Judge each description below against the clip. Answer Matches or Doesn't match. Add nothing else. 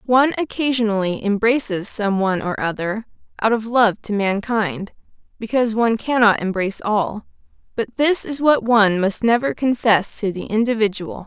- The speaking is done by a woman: Matches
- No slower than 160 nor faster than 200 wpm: Doesn't match